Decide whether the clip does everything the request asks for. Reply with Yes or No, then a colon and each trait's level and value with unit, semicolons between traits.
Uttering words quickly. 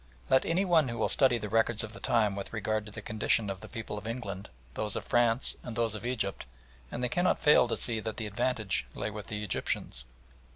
Yes: fast, 235 wpm